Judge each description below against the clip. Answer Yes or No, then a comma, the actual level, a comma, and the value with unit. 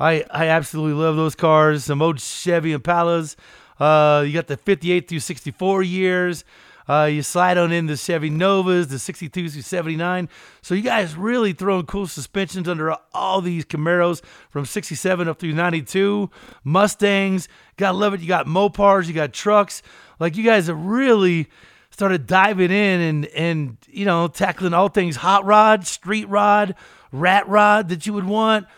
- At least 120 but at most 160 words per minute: No, average, 170 wpm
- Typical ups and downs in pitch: Yes, average, 3.5 semitones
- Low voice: No, medium, 180 Hz